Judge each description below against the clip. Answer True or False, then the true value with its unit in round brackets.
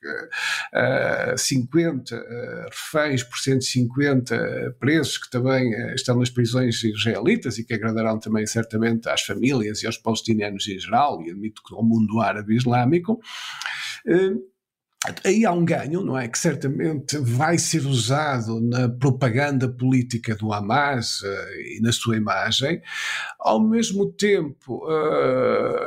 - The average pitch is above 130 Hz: False (125 Hz)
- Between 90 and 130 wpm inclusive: True (125 wpm)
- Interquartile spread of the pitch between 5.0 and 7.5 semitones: True (5.4 semitones)